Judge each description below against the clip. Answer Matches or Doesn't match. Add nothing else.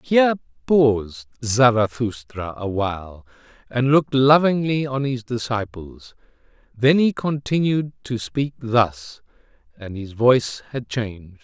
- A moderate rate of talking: Doesn't match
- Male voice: Matches